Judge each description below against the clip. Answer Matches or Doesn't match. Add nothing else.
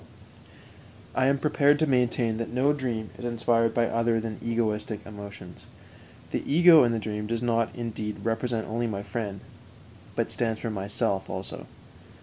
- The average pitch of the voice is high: Doesn't match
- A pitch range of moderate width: Doesn't match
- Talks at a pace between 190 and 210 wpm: Doesn't match